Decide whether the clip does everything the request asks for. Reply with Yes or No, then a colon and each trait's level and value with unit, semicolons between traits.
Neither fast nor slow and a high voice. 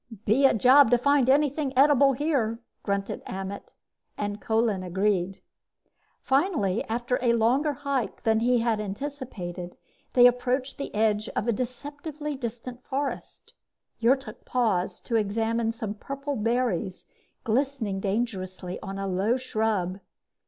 No: slow, 130 wpm; high, 235 Hz